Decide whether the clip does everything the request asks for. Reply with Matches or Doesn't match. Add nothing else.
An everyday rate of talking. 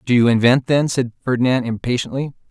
Matches